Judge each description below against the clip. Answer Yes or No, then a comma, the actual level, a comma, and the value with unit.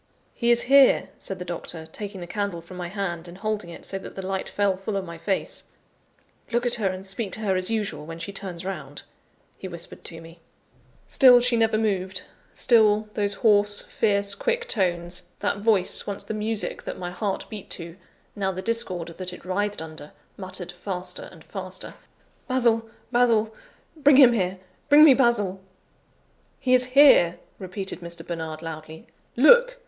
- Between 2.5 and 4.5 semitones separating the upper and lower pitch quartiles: Yes, average, 4.0 semitones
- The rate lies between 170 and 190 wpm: Yes, average, 175 wpm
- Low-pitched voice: No, high, 195 Hz